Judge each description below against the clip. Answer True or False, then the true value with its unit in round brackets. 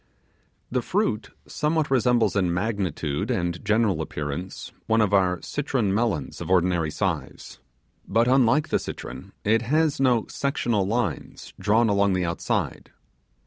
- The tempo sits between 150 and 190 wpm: False (135 wpm)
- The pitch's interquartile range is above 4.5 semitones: True (4.9 semitones)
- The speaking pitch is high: False (105 Hz)